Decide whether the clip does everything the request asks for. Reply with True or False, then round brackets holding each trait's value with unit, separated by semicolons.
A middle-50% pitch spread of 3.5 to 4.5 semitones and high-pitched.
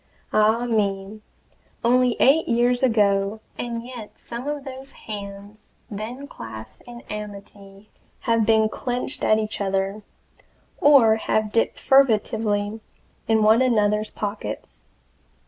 False (2.9 semitones; 220 Hz)